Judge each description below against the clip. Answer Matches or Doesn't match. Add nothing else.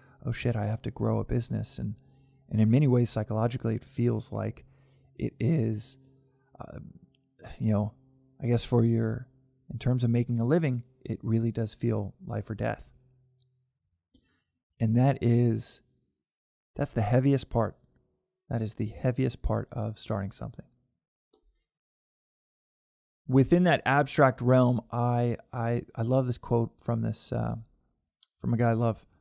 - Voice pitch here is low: Matches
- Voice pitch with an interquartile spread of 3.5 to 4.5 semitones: Doesn't match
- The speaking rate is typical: Matches